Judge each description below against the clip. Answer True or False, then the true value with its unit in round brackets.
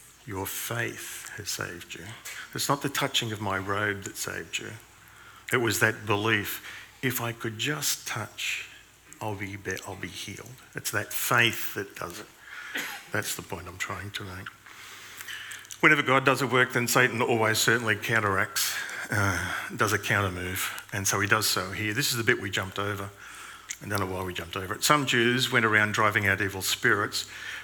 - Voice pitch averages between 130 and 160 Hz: False (105 Hz)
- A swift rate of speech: False (185 wpm)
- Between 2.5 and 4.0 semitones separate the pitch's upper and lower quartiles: True (3.3 semitones)